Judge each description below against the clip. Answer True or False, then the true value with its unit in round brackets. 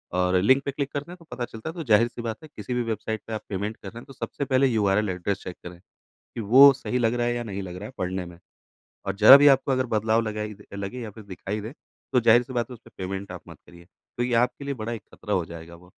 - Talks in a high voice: False (110 Hz)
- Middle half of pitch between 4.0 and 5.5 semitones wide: True (4.4 semitones)